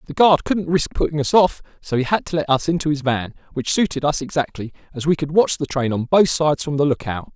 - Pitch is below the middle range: No, medium, 150 Hz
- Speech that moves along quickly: Yes, fast, 270 wpm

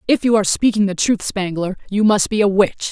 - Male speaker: No, female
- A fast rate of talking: Yes, fast, 245 wpm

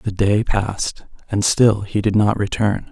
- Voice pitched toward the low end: Yes, low, 105 Hz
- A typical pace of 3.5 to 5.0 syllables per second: Yes, 4.2 syllables/s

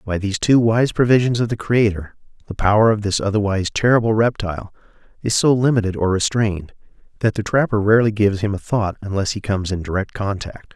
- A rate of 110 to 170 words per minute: No, average, 190 wpm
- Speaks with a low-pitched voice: Yes, low, 105 Hz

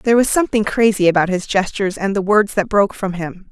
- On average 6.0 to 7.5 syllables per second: Yes, 6.3 syllables/s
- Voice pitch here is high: Yes, high, 200 Hz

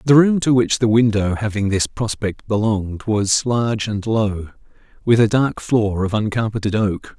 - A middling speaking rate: Yes, average, 175 wpm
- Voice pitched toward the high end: No, low, 110 Hz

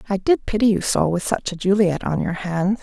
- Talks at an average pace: No, fast, 255 wpm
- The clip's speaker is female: Yes, female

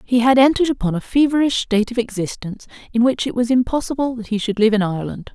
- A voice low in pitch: No, high, 235 Hz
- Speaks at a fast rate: Yes, fast, 225 wpm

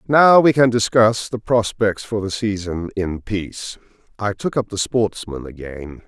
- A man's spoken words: Yes, male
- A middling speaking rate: Yes, average, 170 wpm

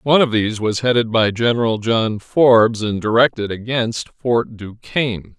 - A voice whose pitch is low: Yes, low, 115 Hz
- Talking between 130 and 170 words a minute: Yes, average, 155 wpm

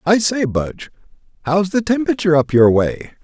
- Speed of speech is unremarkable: Yes, average, 165 wpm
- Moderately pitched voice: Yes, medium, 175 Hz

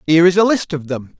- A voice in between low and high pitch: Yes, medium, 165 Hz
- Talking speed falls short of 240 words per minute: No, fast, 300 wpm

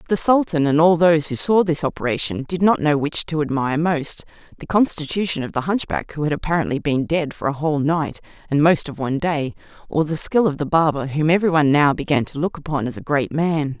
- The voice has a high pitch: No, medium, 155 Hz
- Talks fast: Yes, fast, 225 wpm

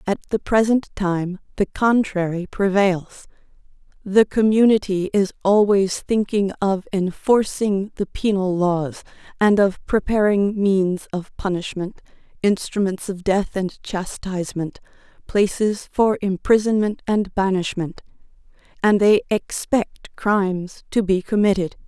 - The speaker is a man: No, female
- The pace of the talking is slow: Yes, slow, 110 wpm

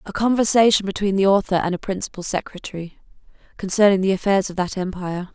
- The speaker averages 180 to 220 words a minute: No, average, 170 wpm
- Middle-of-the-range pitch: No, high, 195 Hz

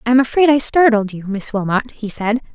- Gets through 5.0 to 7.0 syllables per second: Yes, 5.9 syllables/s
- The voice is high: Yes, high, 230 Hz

